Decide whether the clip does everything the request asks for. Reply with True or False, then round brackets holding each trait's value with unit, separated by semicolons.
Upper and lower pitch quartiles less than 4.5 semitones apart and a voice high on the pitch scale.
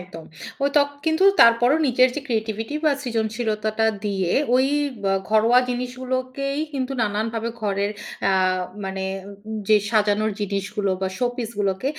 True (3.4 semitones; 225 Hz)